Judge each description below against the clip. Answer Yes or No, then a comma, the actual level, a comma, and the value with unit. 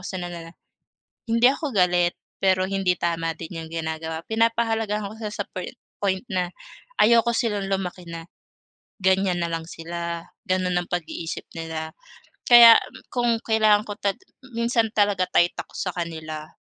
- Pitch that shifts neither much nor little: Yes, average, 4.3 semitones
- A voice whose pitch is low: No, medium, 185 Hz